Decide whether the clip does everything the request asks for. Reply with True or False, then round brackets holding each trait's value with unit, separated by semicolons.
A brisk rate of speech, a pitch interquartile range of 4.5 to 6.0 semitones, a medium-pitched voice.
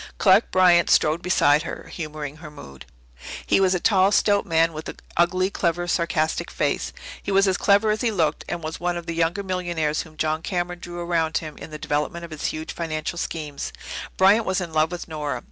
False (210 wpm; 2.9 semitones; 170 Hz)